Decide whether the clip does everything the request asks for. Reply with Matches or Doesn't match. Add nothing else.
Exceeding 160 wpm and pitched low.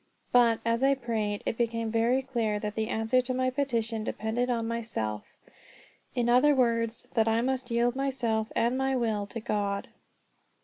Doesn't match